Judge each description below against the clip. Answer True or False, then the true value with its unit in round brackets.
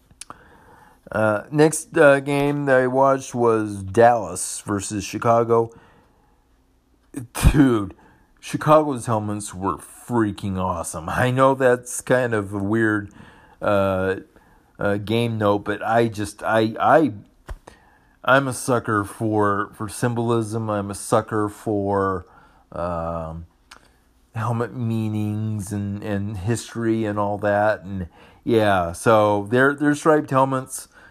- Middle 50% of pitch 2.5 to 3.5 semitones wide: True (3.1 semitones)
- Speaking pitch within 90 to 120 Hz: True (110 Hz)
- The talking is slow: True (115 wpm)